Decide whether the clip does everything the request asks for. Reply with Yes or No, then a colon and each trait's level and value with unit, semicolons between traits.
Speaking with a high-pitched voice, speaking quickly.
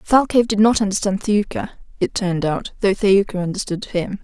No: high, 200 Hz; average, 170 wpm